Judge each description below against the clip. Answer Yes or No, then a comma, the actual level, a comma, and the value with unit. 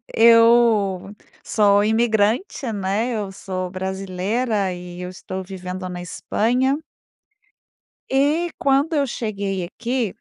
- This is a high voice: Yes, high, 205 Hz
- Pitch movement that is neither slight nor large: Yes, average, 4.2 semitones